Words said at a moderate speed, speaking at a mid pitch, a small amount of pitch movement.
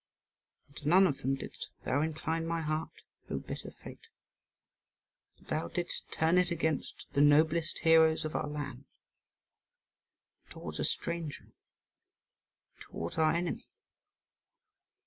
No: slow, 125 wpm; medium, 160 Hz; narrow, 2.0 semitones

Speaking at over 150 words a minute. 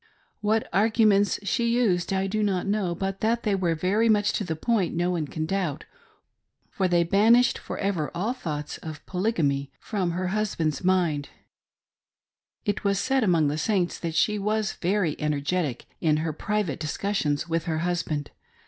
Yes: average, 185 wpm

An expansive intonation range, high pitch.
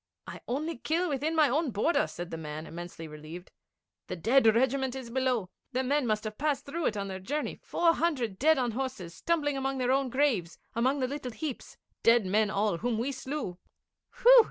Yes: wide, 5.8 semitones; very high, 255 Hz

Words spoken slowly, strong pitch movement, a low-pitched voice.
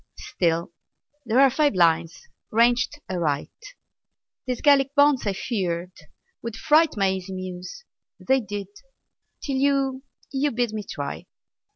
No: slow, 130 wpm; wide, 6.9 semitones; high, 230 Hz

